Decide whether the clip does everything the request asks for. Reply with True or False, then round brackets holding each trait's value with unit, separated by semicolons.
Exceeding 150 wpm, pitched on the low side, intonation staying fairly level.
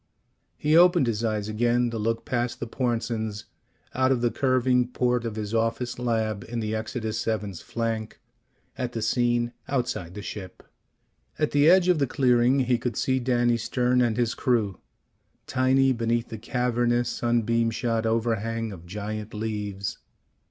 True (160 wpm; 120 Hz; 2.0 semitones)